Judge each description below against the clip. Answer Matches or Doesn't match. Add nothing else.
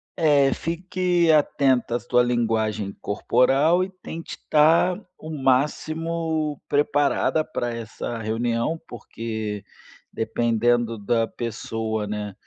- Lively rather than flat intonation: Matches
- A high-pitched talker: Doesn't match